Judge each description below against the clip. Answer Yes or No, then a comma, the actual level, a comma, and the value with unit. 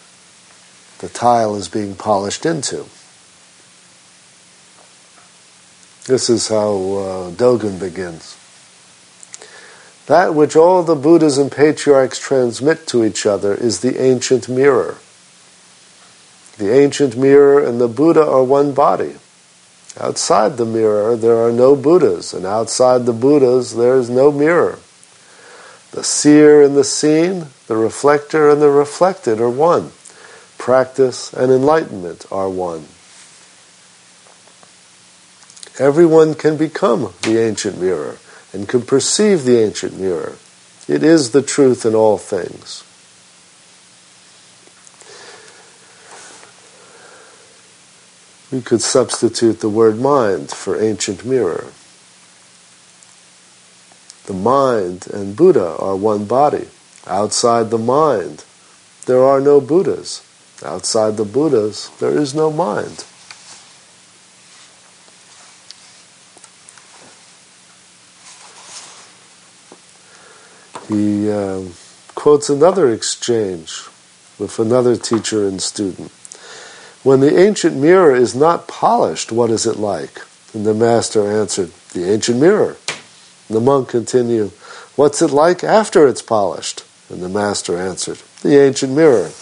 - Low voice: Yes, low, 125 Hz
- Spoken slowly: Yes, slow, 110 wpm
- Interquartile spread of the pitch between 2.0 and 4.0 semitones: No, average, 5.3 semitones